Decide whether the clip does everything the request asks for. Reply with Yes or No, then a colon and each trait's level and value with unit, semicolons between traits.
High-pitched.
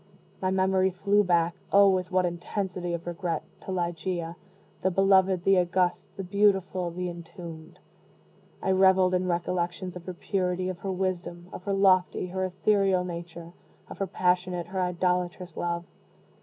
No: medium, 180 Hz